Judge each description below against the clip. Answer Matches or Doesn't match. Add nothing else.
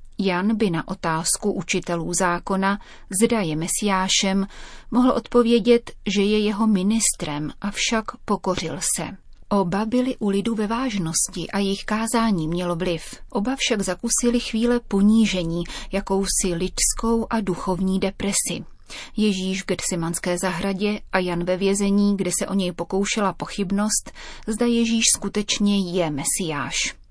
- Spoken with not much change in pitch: Doesn't match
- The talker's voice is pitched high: Matches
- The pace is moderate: Matches